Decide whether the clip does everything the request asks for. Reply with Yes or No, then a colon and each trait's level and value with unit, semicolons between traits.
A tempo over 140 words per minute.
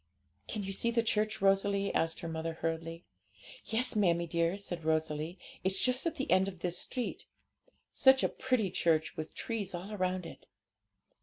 Yes: average, 170 wpm